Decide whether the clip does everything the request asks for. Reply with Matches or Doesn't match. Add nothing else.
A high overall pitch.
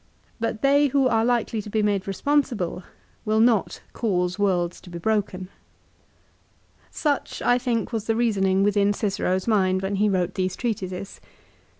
Matches